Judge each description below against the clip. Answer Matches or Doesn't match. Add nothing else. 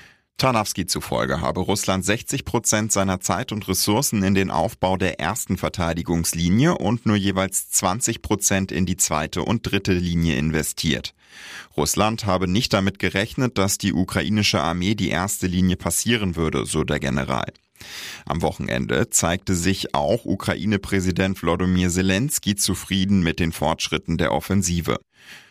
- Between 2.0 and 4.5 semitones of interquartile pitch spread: Matches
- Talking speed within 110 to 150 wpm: Matches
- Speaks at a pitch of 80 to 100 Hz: Matches